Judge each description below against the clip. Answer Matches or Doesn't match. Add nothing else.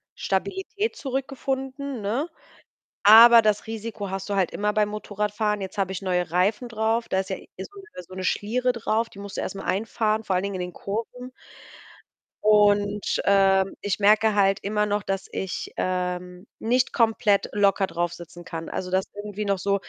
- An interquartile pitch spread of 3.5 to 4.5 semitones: Doesn't match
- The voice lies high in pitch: Matches